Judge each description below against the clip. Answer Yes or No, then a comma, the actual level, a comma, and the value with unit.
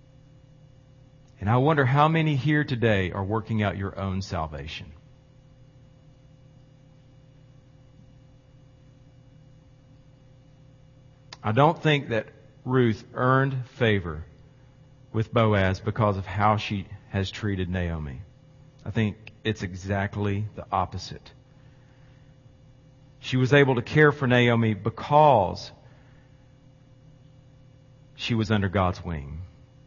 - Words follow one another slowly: Yes, slow, 95 wpm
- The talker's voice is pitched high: No, low, 130 Hz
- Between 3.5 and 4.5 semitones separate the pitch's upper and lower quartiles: Yes, average, 4.0 semitones